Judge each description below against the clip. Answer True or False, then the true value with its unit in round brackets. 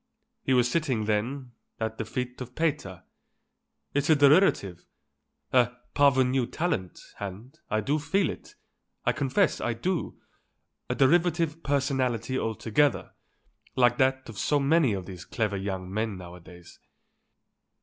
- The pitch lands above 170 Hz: False (125 Hz)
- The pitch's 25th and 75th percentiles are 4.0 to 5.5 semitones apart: True (5.1 semitones)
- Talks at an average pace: False (130 wpm)